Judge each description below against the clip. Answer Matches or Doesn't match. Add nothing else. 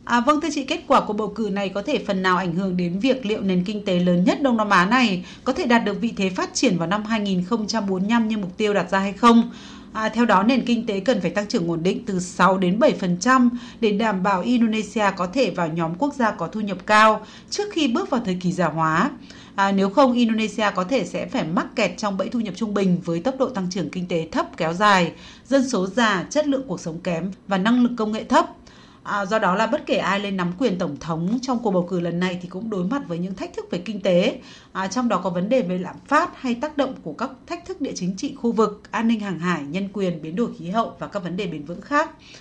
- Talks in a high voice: Matches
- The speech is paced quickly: Matches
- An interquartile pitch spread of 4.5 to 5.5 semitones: Matches